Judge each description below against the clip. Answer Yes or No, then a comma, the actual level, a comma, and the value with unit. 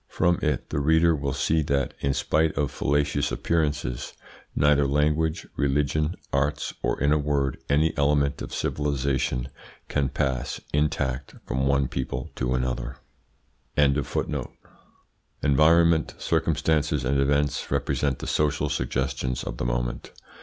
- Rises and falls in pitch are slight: Yes, narrow, 2.2 semitones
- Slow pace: Yes, slow, 125 wpm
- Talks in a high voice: No, very low, 70 Hz